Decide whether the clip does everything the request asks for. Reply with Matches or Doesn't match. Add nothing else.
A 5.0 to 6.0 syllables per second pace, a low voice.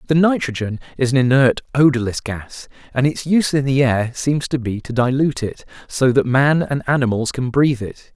Matches